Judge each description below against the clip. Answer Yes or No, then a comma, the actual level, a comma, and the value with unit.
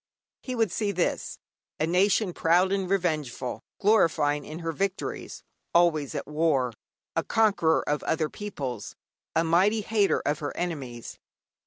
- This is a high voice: No, medium, 165 Hz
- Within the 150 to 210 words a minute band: No, average, 140 wpm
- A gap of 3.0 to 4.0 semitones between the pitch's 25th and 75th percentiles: No, average, 4.9 semitones